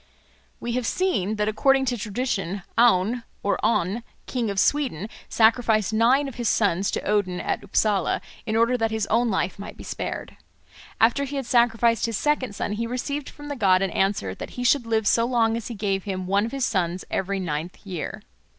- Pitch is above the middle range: Yes, high, 225 Hz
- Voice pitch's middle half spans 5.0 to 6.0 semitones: No, average, 3.7 semitones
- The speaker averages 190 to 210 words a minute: Yes, average, 200 wpm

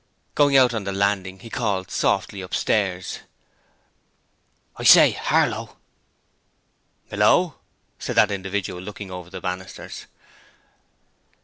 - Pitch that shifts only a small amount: Yes, narrow, 2.3 semitones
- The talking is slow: Yes, slow, 105 wpm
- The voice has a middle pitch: No, low, 100 Hz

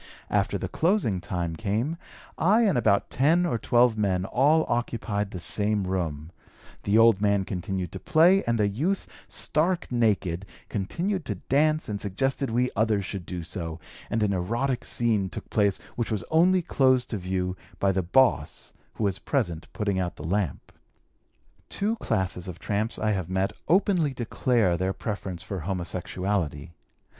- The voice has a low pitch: Yes, low, 105 Hz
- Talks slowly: No, average, 160 wpm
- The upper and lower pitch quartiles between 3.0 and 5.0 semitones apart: No, wide, 5.6 semitones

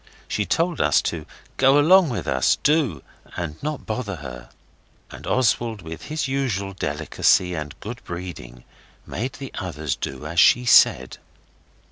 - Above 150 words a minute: No, average, 145 wpm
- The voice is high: No, very low, 95 Hz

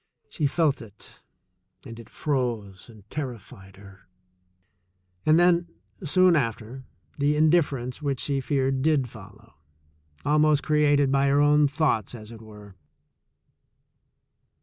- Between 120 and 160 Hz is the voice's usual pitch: Yes, low, 135 Hz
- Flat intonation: No, wide, 5.4 semitones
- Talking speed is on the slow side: Yes, slow, 125 wpm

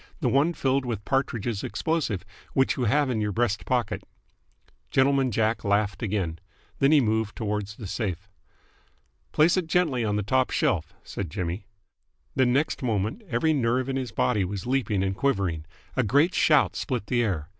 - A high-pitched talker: No, low, 115 Hz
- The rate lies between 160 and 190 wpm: Yes, average, 170 wpm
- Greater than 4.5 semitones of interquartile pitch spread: Yes, average, 4.9 semitones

